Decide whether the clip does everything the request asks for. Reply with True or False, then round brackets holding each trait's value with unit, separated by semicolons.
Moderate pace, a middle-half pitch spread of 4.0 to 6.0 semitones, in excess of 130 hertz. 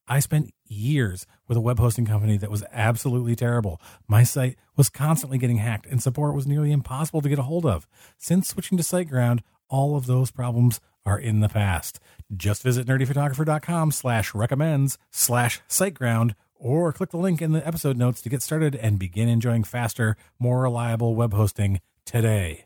False (165 wpm; 4.6 semitones; 120 Hz)